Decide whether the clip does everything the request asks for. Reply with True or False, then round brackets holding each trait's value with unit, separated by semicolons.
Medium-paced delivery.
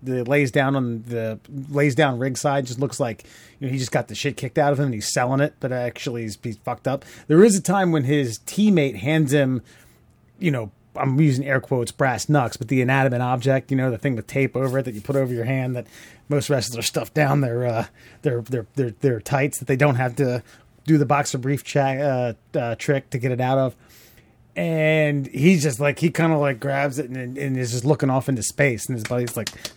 False (245 wpm)